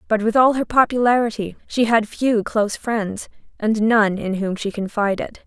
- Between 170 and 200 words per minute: Yes, average, 185 wpm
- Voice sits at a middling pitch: No, high, 220 Hz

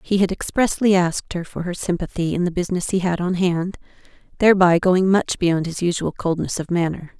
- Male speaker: No, female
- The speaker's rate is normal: Yes, average, 190 wpm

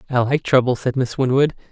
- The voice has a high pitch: No, low, 130 Hz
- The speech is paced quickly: Yes, fast, 210 wpm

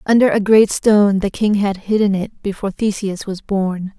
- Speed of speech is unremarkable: Yes, average, 195 wpm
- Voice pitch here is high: Yes, high, 200 Hz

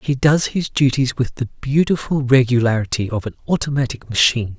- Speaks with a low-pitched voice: Yes, low, 125 Hz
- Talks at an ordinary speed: Yes, average, 155 wpm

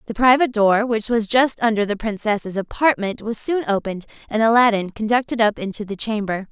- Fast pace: No, average, 185 wpm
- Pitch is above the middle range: Yes, high, 220 Hz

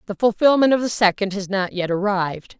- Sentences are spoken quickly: Yes, fast, 210 wpm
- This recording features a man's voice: No, female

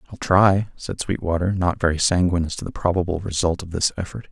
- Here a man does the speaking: Yes, male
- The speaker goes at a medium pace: No, fast, 210 wpm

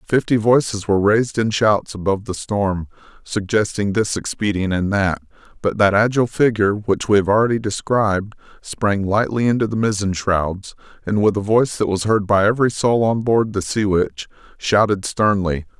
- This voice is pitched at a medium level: No, low, 105 Hz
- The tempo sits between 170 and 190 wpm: Yes, average, 175 wpm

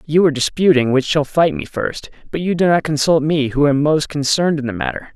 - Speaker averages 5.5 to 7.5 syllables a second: Yes, 5.8 syllables/s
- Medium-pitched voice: Yes, medium, 150 Hz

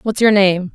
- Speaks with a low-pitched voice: No, high, 200 Hz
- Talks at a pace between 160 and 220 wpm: No, fast, 240 wpm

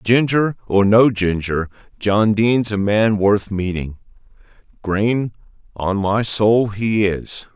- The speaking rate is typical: No, slow, 125 wpm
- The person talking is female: No, male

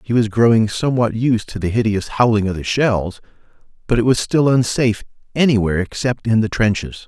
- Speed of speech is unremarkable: Yes, average, 185 wpm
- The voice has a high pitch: No, low, 110 Hz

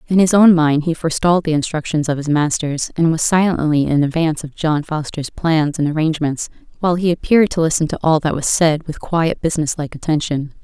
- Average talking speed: No, fast, 210 wpm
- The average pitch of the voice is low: No, medium, 160 Hz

